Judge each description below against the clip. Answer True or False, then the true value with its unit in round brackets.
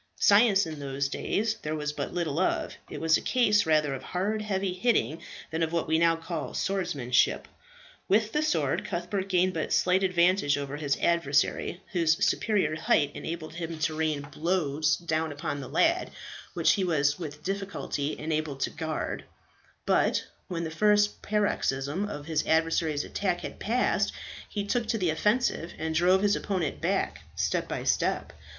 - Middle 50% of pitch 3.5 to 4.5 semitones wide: True (4.1 semitones)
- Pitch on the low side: False (165 Hz)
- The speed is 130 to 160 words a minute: False (170 wpm)